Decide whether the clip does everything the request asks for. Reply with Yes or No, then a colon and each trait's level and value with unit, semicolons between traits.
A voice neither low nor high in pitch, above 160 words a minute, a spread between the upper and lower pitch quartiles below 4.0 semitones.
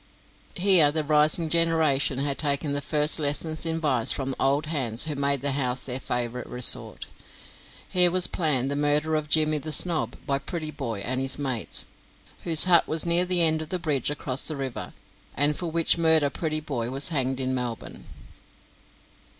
Yes: medium, 145 Hz; average, 175 wpm; average, 3.0 semitones